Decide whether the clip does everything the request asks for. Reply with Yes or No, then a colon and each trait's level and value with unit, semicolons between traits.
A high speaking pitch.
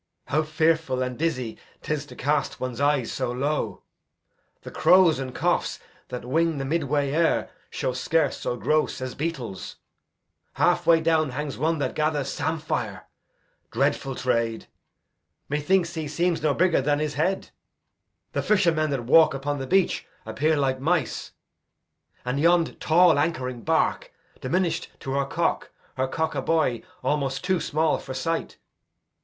No: medium, 150 Hz